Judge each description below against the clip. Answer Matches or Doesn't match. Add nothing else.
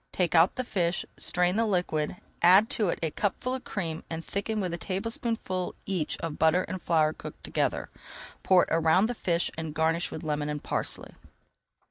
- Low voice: Doesn't match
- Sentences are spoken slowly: Doesn't match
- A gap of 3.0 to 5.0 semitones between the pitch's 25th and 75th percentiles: Matches